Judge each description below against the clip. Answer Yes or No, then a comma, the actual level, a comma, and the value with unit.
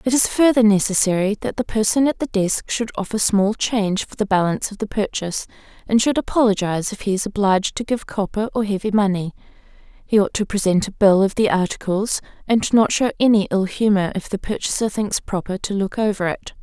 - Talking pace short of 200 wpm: No, fast, 205 wpm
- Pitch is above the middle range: Yes, high, 205 Hz